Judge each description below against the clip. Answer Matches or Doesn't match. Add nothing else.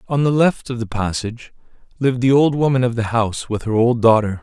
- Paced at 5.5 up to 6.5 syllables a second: Matches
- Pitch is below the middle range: Matches